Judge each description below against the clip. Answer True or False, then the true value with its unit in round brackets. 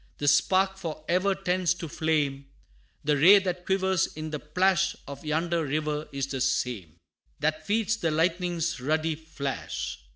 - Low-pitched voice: False (160 Hz)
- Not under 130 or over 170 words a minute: True (155 wpm)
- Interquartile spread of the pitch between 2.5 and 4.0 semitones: True (3.5 semitones)